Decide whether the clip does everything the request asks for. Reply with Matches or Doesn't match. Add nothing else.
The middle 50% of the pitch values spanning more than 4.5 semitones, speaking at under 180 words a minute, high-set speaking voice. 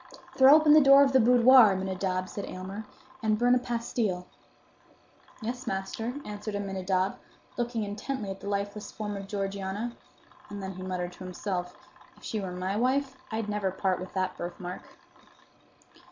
Doesn't match